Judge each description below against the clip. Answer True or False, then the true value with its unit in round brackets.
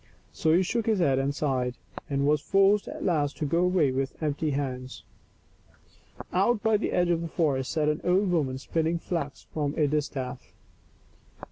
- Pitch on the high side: False (150 Hz)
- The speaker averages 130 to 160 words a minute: False (175 wpm)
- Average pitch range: True (4.3 semitones)